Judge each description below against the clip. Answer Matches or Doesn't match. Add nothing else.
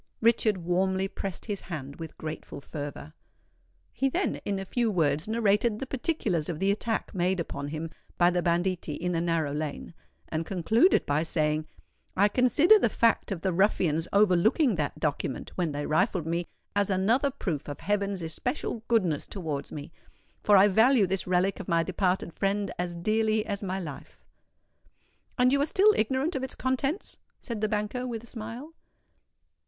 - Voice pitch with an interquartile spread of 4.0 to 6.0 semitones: Matches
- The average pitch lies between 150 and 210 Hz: Matches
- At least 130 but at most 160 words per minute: Doesn't match